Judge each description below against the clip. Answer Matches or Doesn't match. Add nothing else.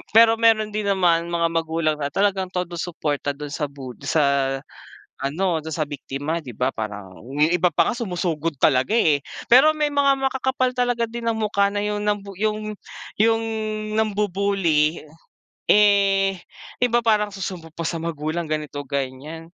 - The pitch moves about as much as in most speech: Doesn't match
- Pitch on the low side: Doesn't match